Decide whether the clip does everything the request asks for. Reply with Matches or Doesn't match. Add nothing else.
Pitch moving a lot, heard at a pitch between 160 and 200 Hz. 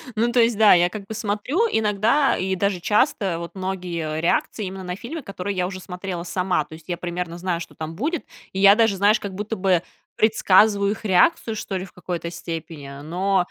Doesn't match